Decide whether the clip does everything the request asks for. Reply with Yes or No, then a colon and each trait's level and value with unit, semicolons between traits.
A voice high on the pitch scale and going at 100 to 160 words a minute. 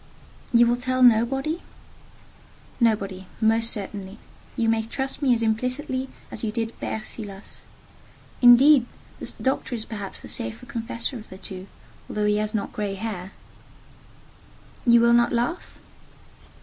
Yes: high, 230 Hz; slow, 135 wpm